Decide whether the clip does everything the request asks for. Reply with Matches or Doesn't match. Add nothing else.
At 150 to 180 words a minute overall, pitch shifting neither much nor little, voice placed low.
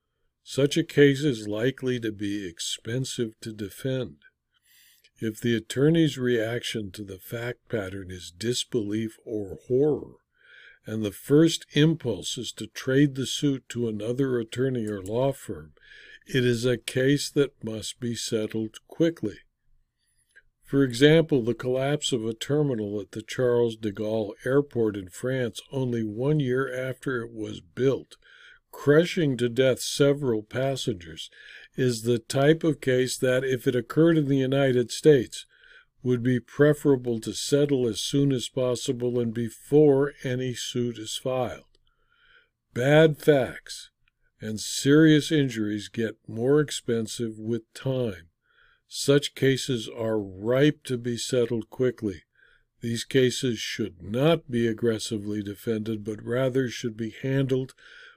Doesn't match